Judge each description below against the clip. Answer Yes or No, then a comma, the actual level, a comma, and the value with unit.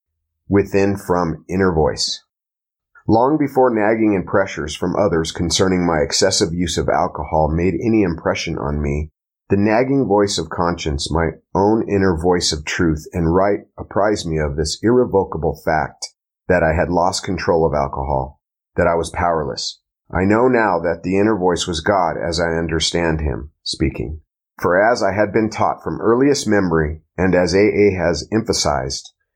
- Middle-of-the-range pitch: No, very low, 90 Hz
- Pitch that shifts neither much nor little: Yes, average, 3.9 semitones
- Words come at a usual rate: Yes, average, 165 wpm